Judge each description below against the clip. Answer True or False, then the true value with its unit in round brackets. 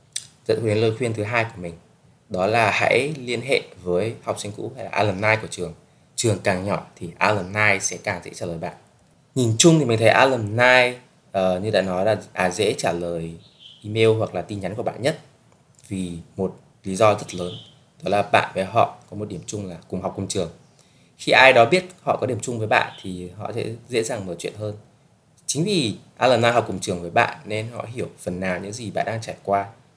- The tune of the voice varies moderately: True (4.3 semitones)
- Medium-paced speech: True (225 wpm)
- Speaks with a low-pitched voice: True (110 Hz)